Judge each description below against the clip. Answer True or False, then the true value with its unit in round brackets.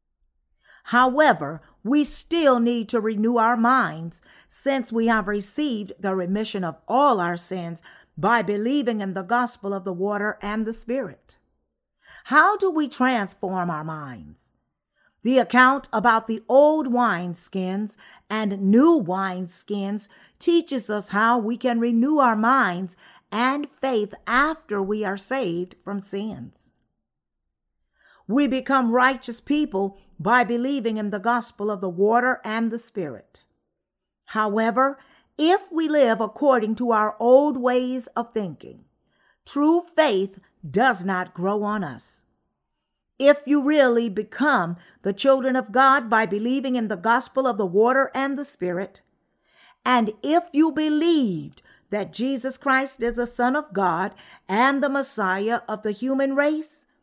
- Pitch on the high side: True (235 Hz)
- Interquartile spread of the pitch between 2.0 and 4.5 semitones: False (5.0 semitones)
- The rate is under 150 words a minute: True (140 wpm)